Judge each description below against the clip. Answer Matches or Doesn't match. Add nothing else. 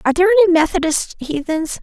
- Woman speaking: Matches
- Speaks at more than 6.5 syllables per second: Matches